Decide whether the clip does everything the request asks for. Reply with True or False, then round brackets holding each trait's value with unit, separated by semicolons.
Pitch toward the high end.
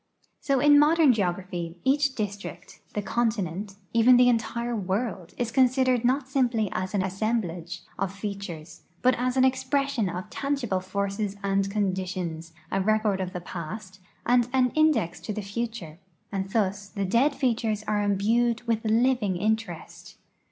True (215 Hz)